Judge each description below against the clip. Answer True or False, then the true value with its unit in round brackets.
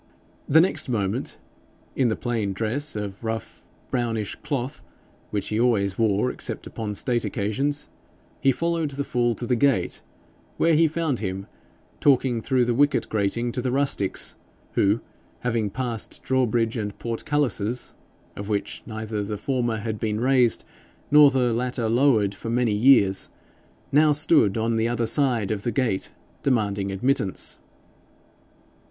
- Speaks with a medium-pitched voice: False (120 Hz)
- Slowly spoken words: False (145 wpm)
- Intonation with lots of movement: False (3.9 semitones)